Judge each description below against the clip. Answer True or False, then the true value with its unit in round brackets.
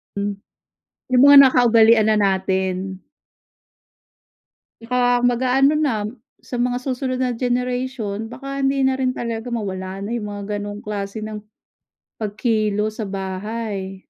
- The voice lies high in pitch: True (225 Hz)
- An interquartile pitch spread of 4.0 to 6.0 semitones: False (3.6 semitones)